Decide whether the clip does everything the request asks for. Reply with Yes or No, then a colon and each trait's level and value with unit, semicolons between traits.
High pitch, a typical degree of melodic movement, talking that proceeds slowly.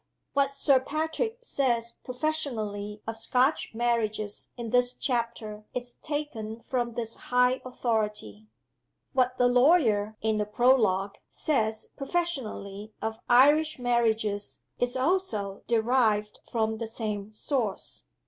Yes: high, 235 Hz; average, 3.4 semitones; slow, 115 wpm